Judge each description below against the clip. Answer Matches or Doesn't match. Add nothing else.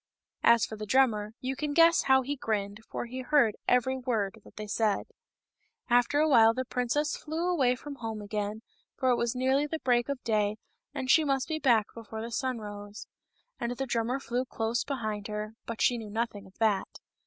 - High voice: Matches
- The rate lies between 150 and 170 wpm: Doesn't match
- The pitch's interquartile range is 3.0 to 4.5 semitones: Matches